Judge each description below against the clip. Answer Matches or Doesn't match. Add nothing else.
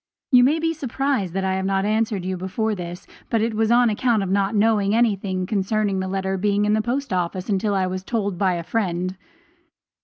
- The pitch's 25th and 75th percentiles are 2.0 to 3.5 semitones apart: Matches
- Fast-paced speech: Matches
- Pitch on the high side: Matches